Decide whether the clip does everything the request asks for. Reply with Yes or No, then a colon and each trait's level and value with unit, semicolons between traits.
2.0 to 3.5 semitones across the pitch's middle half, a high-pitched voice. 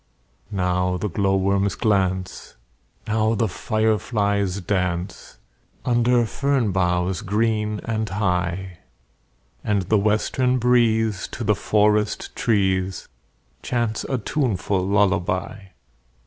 No: average, 2.9 semitones; low, 100 Hz